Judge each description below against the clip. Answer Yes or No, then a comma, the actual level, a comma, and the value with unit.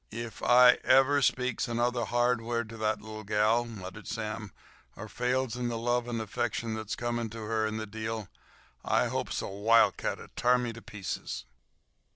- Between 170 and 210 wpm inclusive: Yes, average, 175 wpm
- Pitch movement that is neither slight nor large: No, narrow, 1.9 semitones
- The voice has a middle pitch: No, low, 115 Hz